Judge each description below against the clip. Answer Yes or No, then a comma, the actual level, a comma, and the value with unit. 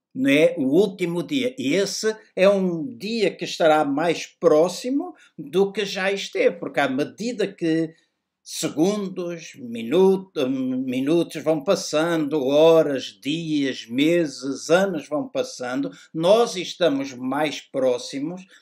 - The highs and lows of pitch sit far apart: Yes, wide, 8.0 semitones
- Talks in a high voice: Yes, high, 195 Hz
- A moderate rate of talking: No, slow, 115 wpm